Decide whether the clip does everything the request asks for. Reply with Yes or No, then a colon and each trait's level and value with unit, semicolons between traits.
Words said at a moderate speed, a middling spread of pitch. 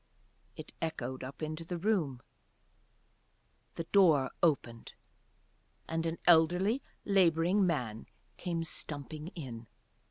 No: slow, 100 wpm; average, 4.1 semitones